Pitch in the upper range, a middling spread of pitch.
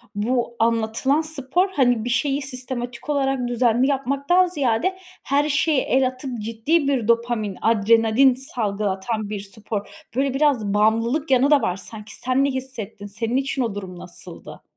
Yes: high, 245 Hz; average, 3.9 semitones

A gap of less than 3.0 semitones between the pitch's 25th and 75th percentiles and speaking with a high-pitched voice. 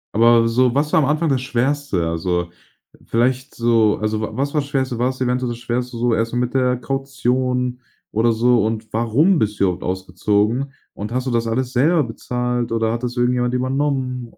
No: narrow, 2.4 semitones; low, 125 Hz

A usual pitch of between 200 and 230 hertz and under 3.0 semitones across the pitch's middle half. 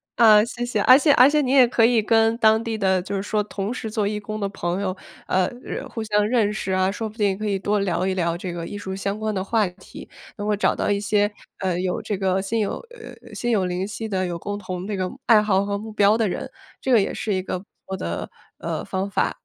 Yes: high, 205 Hz; narrow, 2.6 semitones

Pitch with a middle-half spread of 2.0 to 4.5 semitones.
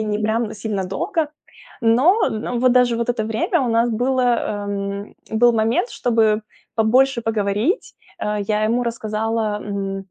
Yes: narrow, 2.4 semitones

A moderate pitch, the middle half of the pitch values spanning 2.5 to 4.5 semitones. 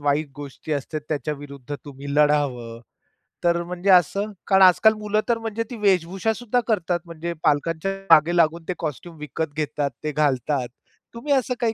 No: medium, 165 Hz; average, 5.0 semitones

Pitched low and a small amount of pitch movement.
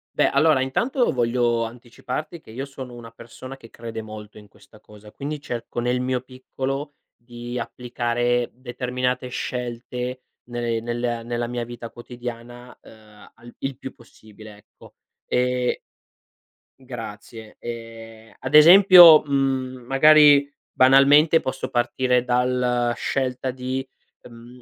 Yes: low, 125 Hz; narrow, 1.9 semitones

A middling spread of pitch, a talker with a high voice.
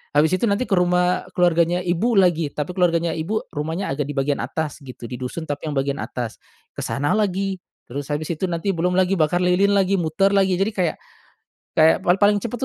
No: average, 4.0 semitones; medium, 175 Hz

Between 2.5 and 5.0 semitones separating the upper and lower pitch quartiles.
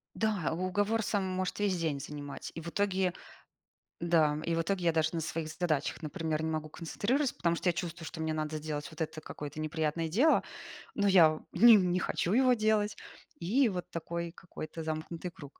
Yes: average, 3.4 semitones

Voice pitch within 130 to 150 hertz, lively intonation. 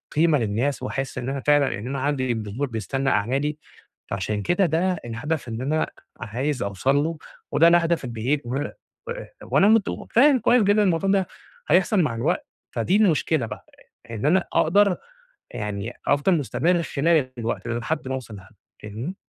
Yes: medium, 140 Hz; wide, 6.4 semitones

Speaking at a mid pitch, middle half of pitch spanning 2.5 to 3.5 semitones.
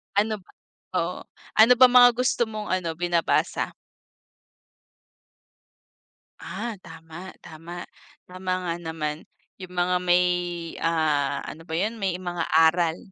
Yes: medium, 175 Hz; average, 3.0 semitones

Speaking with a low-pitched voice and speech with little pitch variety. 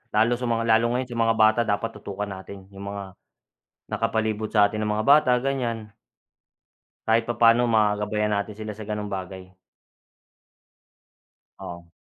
Yes: low, 110 Hz; narrow, 2.1 semitones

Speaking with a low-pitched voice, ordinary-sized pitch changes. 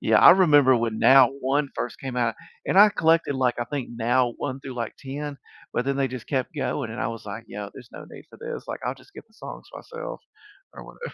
Yes: low, 130 Hz; average, 3.5 semitones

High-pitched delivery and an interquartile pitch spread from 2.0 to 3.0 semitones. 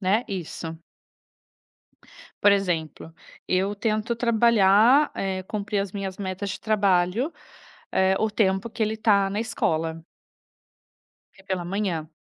Yes: high, 195 Hz; narrow, 2.5 semitones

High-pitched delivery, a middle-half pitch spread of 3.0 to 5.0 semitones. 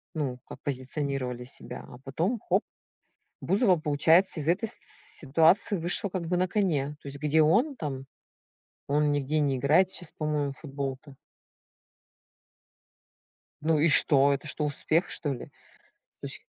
No: medium, 150 Hz; average, 3.7 semitones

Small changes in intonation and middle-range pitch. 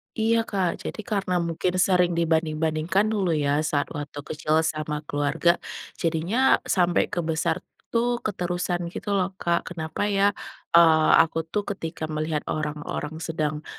No: average, 3.4 semitones; medium, 170 Hz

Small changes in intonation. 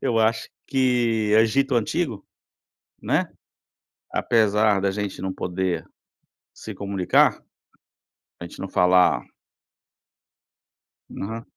No: average, 3.1 semitones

